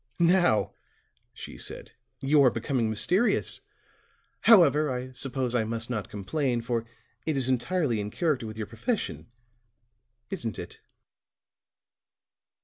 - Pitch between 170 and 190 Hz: No, low, 125 Hz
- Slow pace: Yes, slow, 120 wpm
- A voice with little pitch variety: No, average, 5.1 semitones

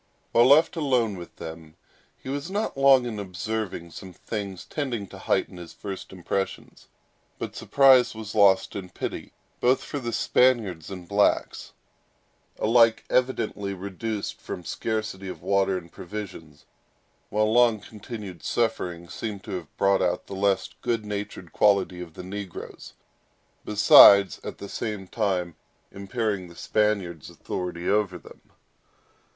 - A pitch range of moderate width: Yes, average, 3.6 semitones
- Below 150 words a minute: Yes, average, 140 wpm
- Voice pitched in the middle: No, low, 100 Hz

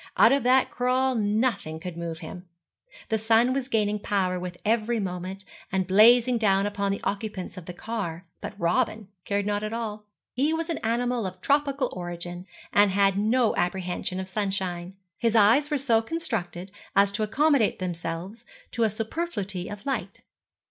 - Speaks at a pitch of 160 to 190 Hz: No, high, 205 Hz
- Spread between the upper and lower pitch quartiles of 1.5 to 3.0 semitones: No, average, 4.2 semitones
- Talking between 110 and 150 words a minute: No, average, 170 wpm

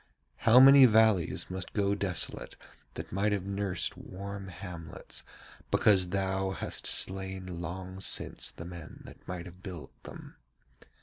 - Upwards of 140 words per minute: No, slow, 135 wpm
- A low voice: Yes, very low, 95 Hz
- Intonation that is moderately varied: No, narrow, 1.8 semitones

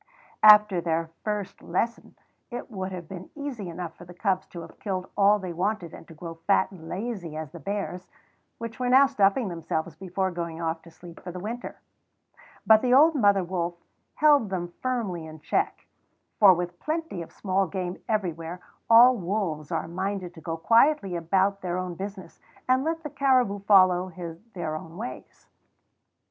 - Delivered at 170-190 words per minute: Yes, average, 175 wpm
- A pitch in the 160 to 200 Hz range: Yes, high, 190 Hz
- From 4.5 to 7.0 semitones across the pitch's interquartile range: No, average, 4.0 semitones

